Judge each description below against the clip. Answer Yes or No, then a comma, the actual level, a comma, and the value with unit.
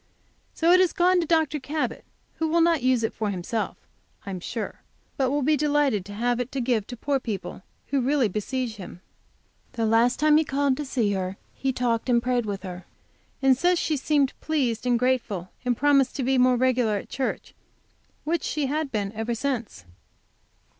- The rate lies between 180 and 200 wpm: Yes, average, 195 wpm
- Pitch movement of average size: Yes, average, 4.5 semitones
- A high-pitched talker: Yes, very high, 255 Hz